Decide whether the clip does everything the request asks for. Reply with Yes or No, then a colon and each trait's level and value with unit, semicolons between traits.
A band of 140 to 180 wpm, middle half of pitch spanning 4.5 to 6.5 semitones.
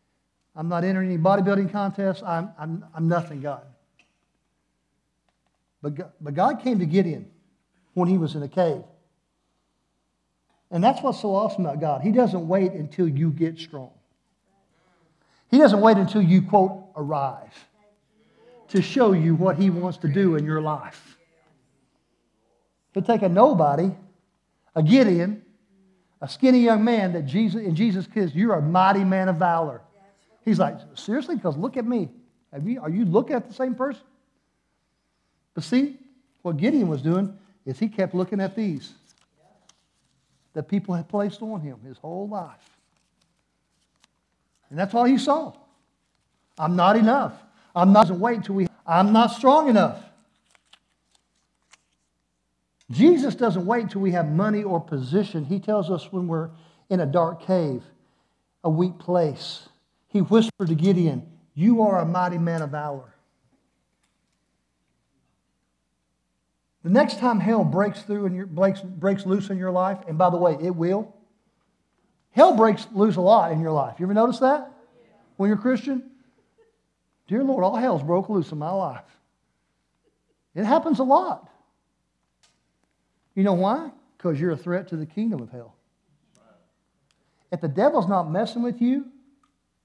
Yes: average, 150 wpm; average, 5.2 semitones